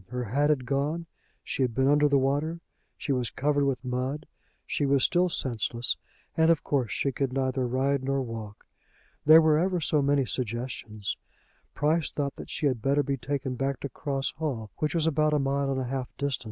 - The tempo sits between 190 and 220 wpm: Yes, average, 200 wpm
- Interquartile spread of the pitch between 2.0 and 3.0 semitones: Yes, narrow, 2.5 semitones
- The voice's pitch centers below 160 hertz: Yes, low, 135 Hz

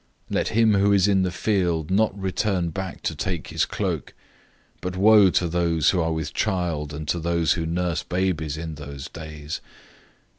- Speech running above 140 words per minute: Yes, average, 190 wpm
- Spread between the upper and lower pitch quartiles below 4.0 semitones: Yes, average, 3.1 semitones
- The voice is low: Yes, very low, 85 Hz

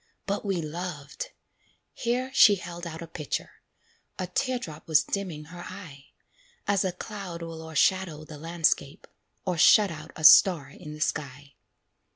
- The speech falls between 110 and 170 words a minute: Yes, average, 155 wpm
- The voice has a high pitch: No, medium, 170 Hz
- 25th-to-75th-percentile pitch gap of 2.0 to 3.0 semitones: No, average, 3.8 semitones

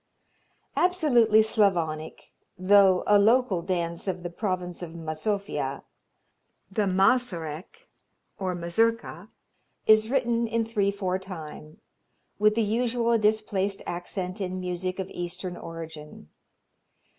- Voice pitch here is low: No, high, 190 Hz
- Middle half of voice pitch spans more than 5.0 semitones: No, average, 3.8 semitones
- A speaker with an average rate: No, slow, 110 wpm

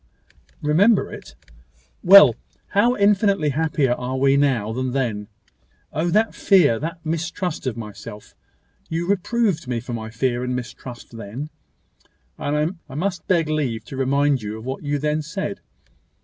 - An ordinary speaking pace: Yes, average, 150 wpm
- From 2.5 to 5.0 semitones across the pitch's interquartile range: No, wide, 5.4 semitones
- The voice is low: No, medium, 145 Hz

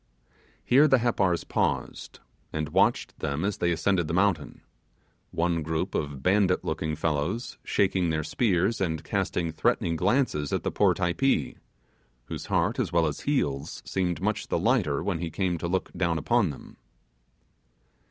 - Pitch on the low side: Yes, very low, 85 Hz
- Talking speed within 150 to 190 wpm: Yes, average, 155 wpm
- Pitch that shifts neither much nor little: Yes, average, 4.1 semitones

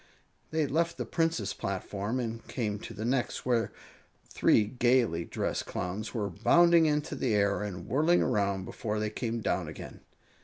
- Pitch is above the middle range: No, low, 115 Hz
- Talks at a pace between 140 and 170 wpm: Yes, average, 160 wpm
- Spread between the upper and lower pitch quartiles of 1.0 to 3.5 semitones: No, average, 4.6 semitones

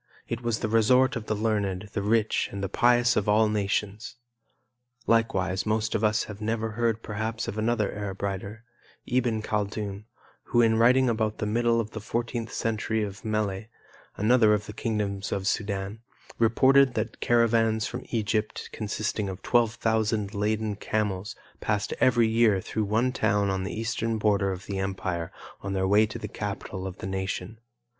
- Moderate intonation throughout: No, narrow, 2.1 semitones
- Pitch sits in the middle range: No, low, 110 Hz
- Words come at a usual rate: Yes, average, 175 wpm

